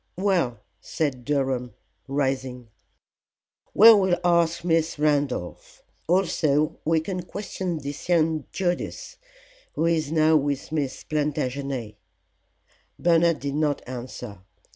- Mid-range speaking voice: Yes, medium, 155 Hz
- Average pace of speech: No, slow, 105 wpm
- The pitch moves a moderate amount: Yes, average, 3.8 semitones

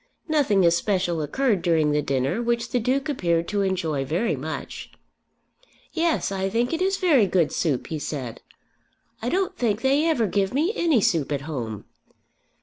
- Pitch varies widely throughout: Yes, wide, 8.6 semitones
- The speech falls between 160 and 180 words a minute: Yes, average, 165 wpm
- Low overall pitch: No, high, 195 Hz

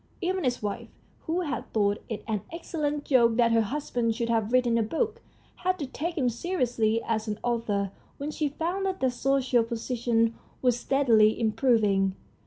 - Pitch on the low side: No, high, 240 Hz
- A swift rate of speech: No, average, 175 wpm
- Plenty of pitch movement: No, average, 4.6 semitones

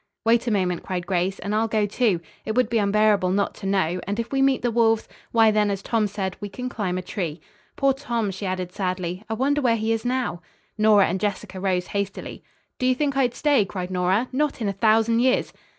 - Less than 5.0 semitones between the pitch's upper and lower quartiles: Yes, average, 3.7 semitones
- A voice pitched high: Yes, high, 210 Hz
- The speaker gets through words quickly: Yes, fast, 230 wpm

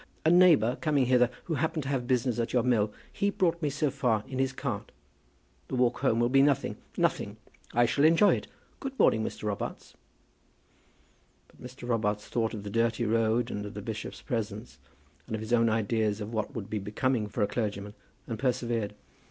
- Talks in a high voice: No, low, 120 Hz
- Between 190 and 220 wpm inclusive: Yes, average, 195 wpm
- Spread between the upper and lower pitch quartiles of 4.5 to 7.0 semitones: No, average, 3.5 semitones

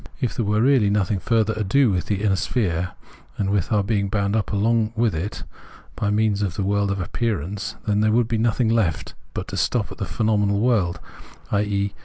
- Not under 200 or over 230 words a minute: Yes, fast, 205 wpm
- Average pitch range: No, narrow, 2.1 semitones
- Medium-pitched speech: No, low, 105 Hz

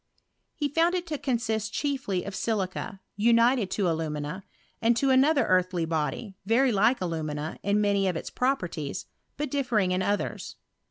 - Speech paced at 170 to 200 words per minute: No, average, 155 wpm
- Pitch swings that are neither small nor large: No, wide, 5.9 semitones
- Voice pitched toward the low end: No, high, 210 Hz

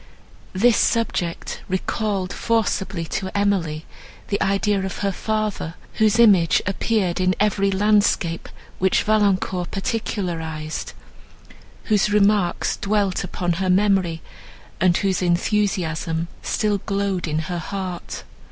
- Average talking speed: No, slow, 110 wpm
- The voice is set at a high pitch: Yes, high, 195 Hz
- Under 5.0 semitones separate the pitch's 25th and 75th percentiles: Yes, average, 3.0 semitones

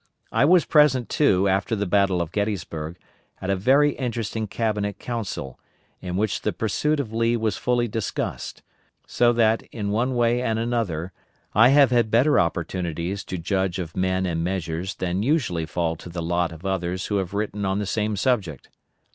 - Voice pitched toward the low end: Yes, low, 100 Hz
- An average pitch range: Yes, average, 4.7 semitones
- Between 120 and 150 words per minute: No, average, 180 wpm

